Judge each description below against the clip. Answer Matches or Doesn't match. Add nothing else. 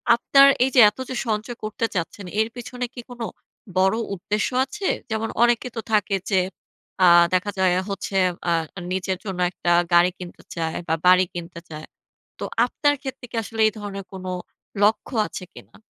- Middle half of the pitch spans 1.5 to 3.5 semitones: Doesn't match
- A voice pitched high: Matches